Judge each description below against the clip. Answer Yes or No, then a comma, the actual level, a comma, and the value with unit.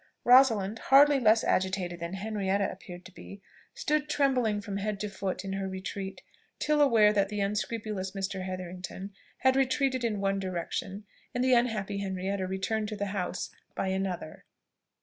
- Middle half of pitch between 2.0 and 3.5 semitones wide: Yes, average, 2.9 semitones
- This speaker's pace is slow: No, average, 160 wpm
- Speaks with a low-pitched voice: No, high, 200 Hz